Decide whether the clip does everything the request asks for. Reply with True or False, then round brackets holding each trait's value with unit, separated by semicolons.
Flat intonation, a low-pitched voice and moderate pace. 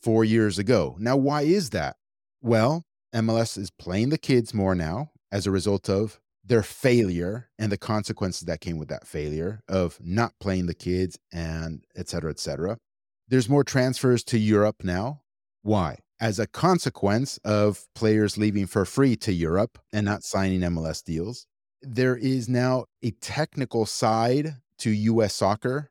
False (4.7 semitones; 105 Hz; 160 wpm)